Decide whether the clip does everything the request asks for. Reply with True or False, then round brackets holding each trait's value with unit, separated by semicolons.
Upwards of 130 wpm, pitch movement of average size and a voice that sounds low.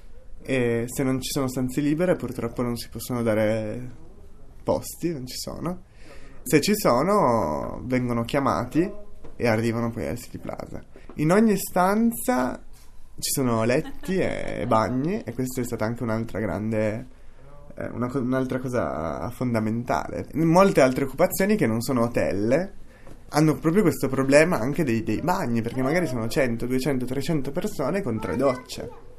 True (150 wpm; 4.7 semitones; 130 Hz)